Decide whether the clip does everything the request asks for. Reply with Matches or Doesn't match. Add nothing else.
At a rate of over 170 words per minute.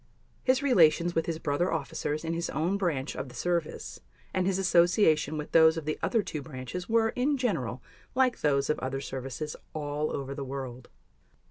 Matches